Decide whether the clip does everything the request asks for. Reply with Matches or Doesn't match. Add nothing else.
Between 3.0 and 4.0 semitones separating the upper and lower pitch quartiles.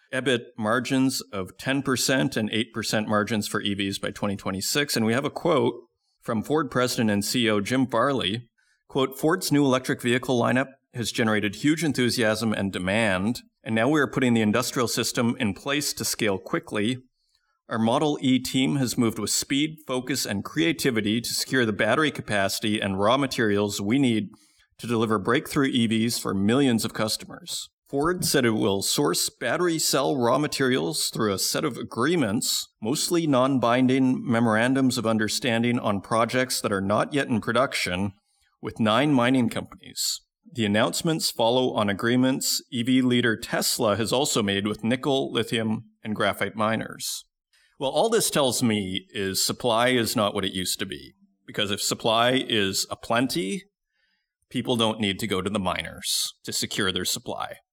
Matches